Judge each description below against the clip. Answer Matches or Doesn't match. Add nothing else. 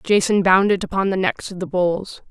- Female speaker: Matches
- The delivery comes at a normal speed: Doesn't match